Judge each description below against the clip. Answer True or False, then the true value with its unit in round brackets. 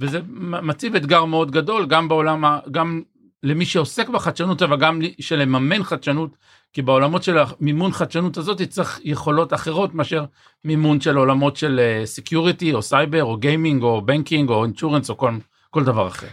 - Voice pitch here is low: False (155 Hz)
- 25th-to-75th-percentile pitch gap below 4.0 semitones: True (2.8 semitones)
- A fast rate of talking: True (160 wpm)